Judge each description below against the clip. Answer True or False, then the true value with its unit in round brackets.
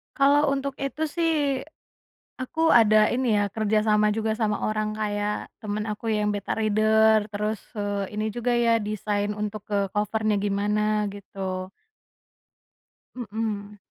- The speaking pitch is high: True (215 Hz)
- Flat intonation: True (1.3 semitones)